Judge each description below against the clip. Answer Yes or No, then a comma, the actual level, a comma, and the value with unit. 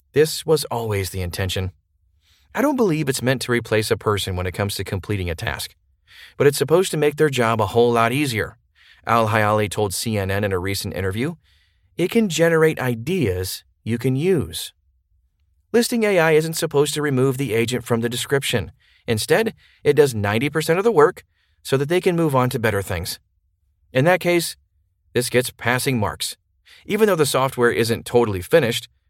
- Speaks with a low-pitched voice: Yes, low, 120 Hz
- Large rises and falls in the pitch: Yes, wide, 7.3 semitones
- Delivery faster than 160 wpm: Yes, average, 180 wpm